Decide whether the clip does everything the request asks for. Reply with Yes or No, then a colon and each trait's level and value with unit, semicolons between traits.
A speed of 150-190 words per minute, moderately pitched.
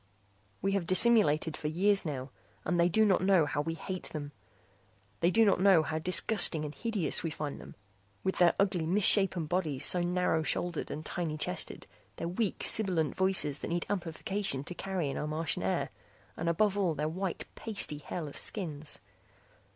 Yes: average, 175 wpm; medium, 175 Hz